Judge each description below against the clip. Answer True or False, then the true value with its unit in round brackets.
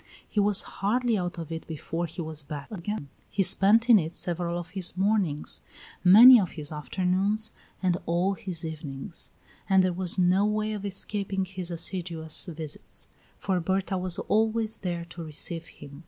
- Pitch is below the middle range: False (180 Hz)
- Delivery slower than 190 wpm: True (170 wpm)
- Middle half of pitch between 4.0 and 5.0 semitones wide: False (3.2 semitones)